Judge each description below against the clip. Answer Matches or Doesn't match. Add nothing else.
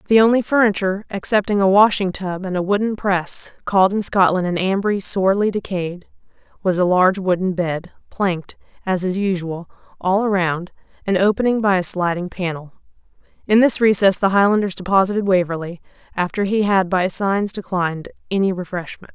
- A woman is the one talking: Matches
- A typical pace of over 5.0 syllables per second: Matches